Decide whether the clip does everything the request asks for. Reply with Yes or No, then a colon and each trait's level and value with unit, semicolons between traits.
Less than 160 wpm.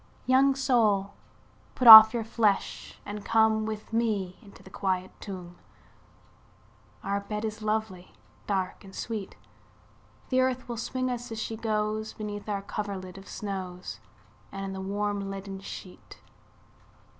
Yes: average, 140 wpm